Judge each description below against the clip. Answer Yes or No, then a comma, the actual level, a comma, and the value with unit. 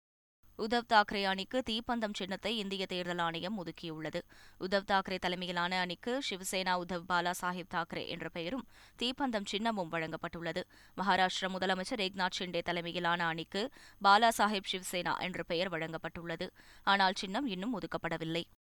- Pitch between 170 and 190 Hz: Yes, medium, 185 Hz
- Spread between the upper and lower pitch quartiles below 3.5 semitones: Yes, average, 2.9 semitones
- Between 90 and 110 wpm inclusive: No, average, 125 wpm